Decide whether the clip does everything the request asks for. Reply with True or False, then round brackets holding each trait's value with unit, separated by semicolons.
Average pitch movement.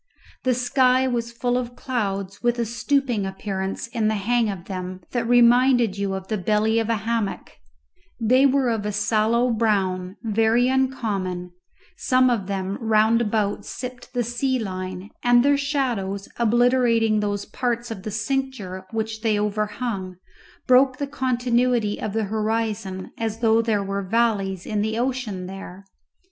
True (3.4 semitones)